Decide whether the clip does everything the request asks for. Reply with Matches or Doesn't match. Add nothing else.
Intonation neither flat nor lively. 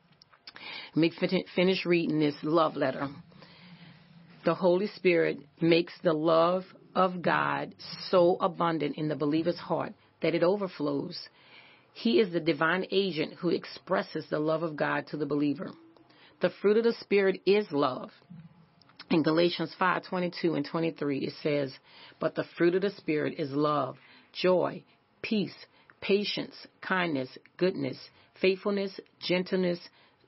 Matches